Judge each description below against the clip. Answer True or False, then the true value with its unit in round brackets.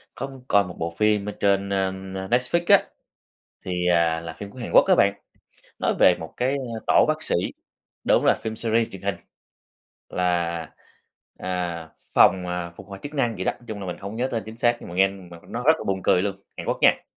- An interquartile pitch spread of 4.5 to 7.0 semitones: False (4.0 semitones)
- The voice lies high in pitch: False (100 Hz)